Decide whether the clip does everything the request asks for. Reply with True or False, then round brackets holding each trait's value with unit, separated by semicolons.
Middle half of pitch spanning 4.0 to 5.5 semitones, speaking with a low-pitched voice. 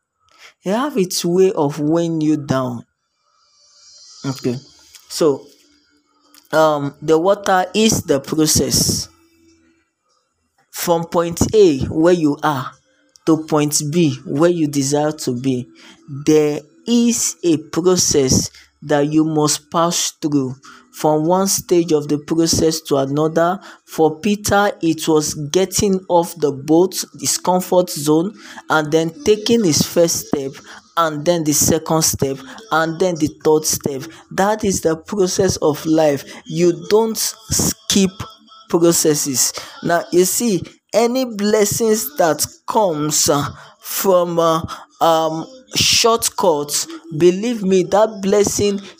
False (4.7 semitones; 165 Hz)